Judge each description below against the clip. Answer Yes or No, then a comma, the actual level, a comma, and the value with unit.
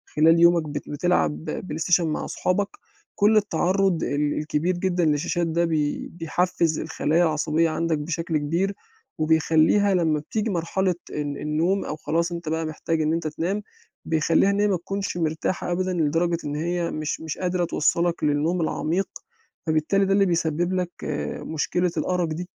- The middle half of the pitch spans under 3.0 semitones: Yes, narrow, 2.5 semitones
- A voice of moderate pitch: Yes, medium, 165 Hz